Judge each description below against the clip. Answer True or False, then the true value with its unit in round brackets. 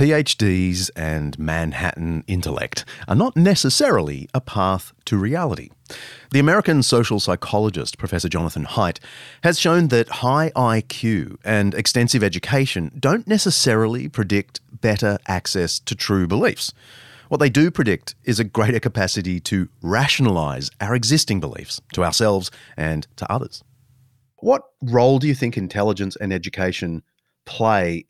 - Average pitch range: False (5.9 semitones)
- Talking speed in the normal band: False (130 wpm)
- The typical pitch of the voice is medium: False (110 Hz)